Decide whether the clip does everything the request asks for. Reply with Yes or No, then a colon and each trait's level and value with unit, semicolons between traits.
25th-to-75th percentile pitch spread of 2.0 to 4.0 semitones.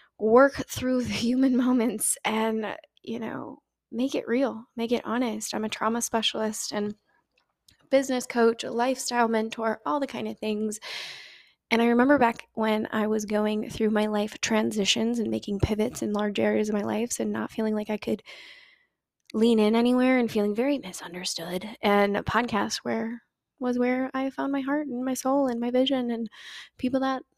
Yes: average, 2.9 semitones